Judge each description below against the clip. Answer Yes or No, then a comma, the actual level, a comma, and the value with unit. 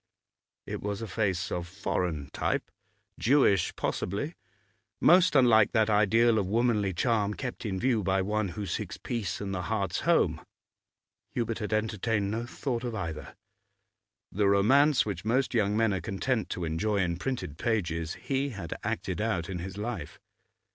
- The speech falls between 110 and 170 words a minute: Yes, average, 160 wpm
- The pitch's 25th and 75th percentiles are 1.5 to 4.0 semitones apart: Yes, average, 3.6 semitones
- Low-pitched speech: Yes, low, 105 Hz